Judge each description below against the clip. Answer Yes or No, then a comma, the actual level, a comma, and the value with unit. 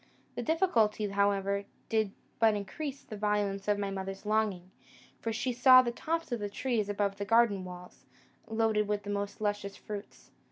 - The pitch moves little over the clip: Yes, narrow, 2.2 semitones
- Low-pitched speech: No, high, 210 Hz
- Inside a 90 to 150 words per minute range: No, average, 170 wpm